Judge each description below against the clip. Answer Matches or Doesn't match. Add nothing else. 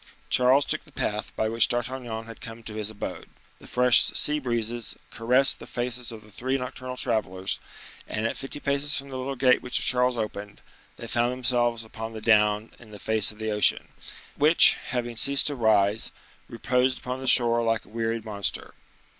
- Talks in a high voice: Doesn't match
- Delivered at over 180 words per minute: Matches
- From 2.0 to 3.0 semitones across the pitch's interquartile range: Matches